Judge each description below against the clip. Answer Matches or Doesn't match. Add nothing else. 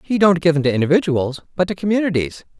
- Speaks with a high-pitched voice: Doesn't match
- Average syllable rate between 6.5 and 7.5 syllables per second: Matches